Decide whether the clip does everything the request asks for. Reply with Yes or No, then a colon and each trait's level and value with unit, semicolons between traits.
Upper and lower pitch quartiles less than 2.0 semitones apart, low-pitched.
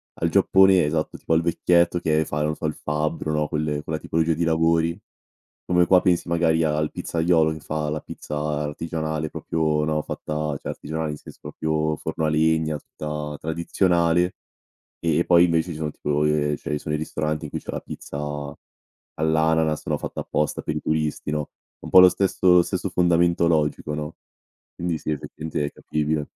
Yes: narrow, 1.6 semitones; very low, 80 Hz